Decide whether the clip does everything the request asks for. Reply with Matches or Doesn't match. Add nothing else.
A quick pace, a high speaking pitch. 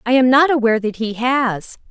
Matches